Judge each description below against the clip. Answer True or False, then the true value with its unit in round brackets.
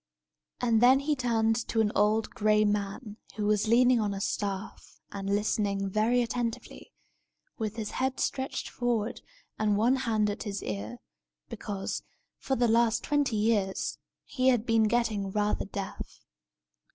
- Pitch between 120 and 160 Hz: False (220 Hz)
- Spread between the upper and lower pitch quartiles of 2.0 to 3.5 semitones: True (2.7 semitones)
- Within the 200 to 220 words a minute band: False (150 wpm)